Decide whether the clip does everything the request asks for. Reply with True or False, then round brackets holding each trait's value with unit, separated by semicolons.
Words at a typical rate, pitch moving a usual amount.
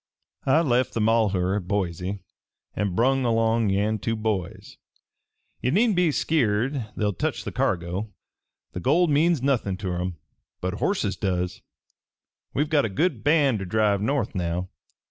False (155 wpm; 6.1 semitones)